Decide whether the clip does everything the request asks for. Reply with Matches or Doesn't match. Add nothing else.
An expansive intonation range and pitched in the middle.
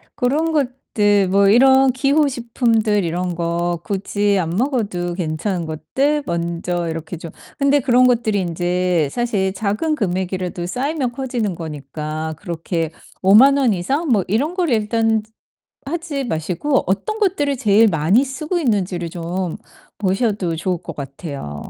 Doesn't match